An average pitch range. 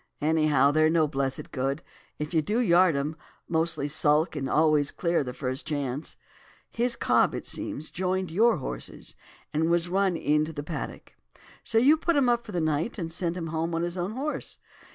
Yes: average, 3.6 semitones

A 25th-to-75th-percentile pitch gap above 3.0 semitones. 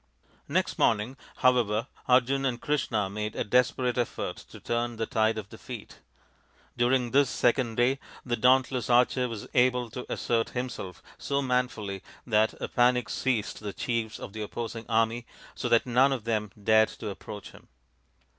No: narrow, 2.5 semitones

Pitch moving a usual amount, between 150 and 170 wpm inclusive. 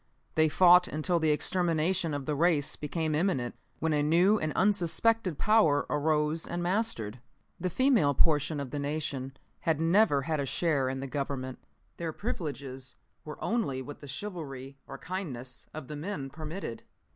Yes: average, 3.9 semitones; average, 160 wpm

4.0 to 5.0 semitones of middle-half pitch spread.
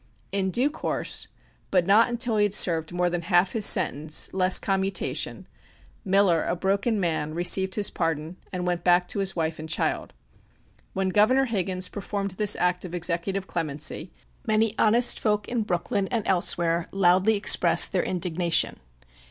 No: average, 2.9 semitones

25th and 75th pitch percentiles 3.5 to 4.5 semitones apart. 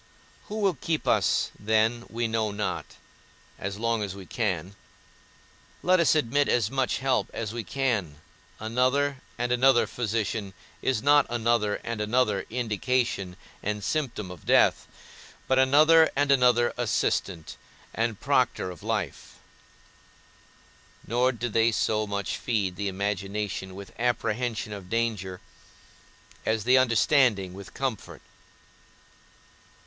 Yes: average, 3.8 semitones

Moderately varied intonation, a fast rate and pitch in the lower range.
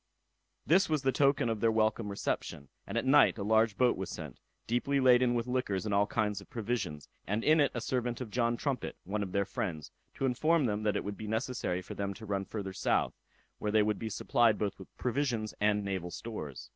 Yes: average, 3.8 semitones; fast, 220 wpm; low, 110 Hz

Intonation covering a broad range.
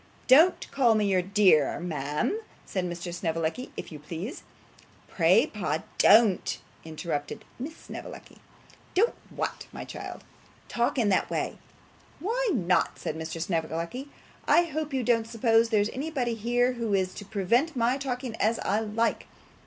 Yes: wide, 6.1 semitones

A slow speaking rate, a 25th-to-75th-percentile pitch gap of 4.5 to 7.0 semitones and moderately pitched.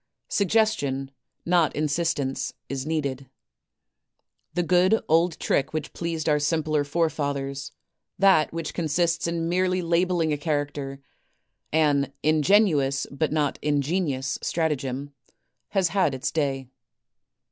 No: slow, 120 wpm; average, 3.3 semitones; medium, 155 Hz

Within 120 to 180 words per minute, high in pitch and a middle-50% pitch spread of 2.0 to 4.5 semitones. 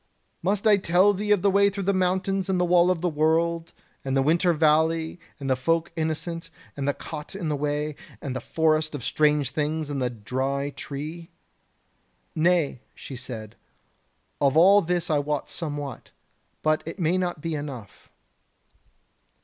No: average, 170 wpm; medium, 160 Hz; average, 3.6 semitones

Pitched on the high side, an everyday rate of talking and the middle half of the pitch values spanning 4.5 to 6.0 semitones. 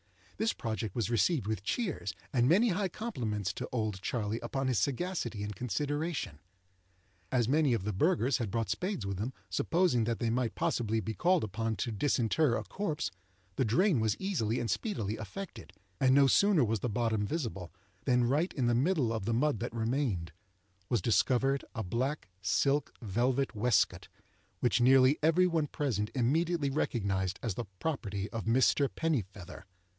No: low, 120 Hz; average, 170 wpm; average, 5.3 semitones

